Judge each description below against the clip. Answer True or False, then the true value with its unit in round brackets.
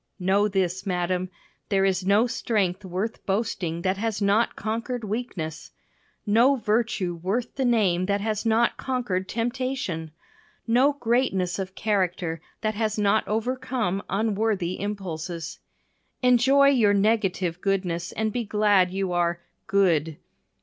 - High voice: True (200 Hz)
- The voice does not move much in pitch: False (3.7 semitones)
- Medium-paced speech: False (130 wpm)